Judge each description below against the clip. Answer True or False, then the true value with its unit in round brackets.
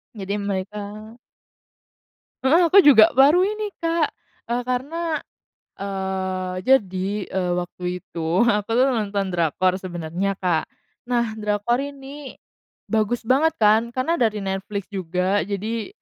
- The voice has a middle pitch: False (210 Hz)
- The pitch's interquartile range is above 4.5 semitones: True (5.6 semitones)